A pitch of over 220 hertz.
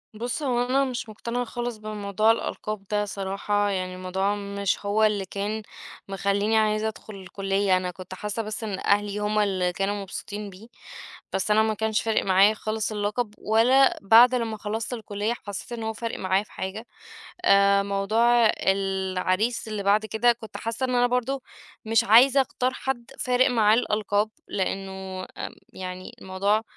No: high, 210 Hz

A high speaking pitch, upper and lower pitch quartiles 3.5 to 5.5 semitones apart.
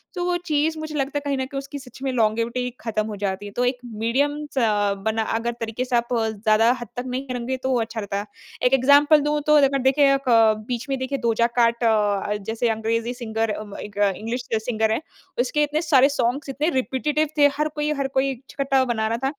Yes: very high, 250 Hz; average, 3.8 semitones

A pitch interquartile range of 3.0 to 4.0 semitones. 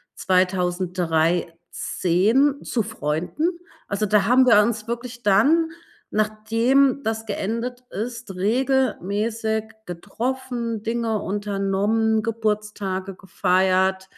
Yes: average, 3.7 semitones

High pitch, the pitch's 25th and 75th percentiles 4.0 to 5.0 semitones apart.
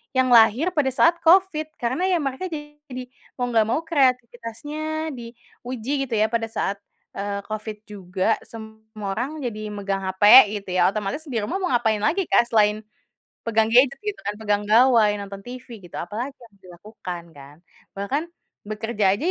Yes: high, 230 Hz; average, 4.7 semitones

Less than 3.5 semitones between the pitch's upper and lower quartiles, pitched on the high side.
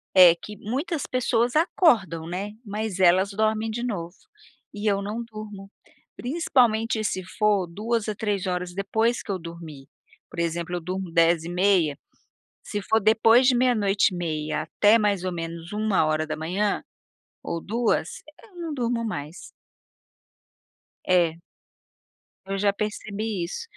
No: average, 4.2 semitones; high, 200 Hz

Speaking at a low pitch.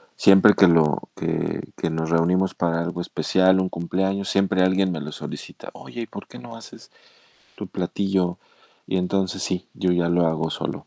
Yes: very low, 90 Hz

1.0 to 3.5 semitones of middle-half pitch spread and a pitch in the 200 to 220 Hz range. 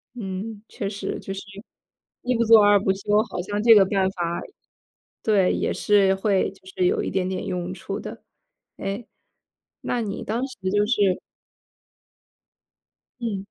Yes: narrow, 2.6 semitones; high, 205 Hz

